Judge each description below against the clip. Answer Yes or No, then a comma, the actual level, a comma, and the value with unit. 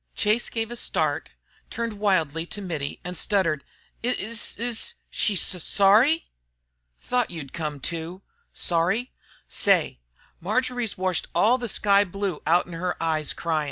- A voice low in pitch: No, high, 195 Hz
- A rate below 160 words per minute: Yes, average, 145 wpm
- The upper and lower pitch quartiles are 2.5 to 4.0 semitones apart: No, average, 5.2 semitones